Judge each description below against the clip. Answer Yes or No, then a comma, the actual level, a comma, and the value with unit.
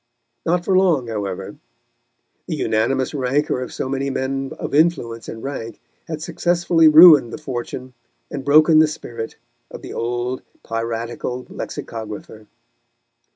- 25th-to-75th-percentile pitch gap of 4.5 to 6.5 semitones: Yes, average, 4.9 semitones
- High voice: No, low, 130 Hz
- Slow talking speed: Yes, slow, 130 wpm